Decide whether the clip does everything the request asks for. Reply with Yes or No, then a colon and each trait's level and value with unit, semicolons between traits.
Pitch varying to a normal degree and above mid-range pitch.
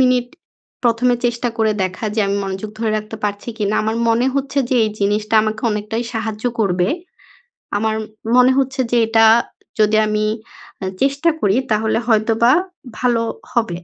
No: narrow, 2.3 semitones; high, 220 Hz